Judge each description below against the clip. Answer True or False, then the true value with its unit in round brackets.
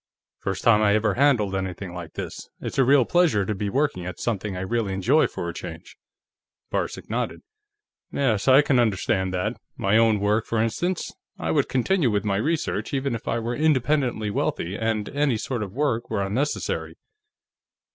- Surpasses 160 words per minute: True (180 wpm)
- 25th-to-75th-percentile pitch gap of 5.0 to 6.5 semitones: True (5.3 semitones)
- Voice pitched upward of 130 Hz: False (115 Hz)